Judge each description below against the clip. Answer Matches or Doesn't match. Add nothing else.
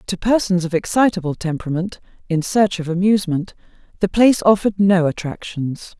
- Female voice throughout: Matches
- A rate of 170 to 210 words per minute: Doesn't match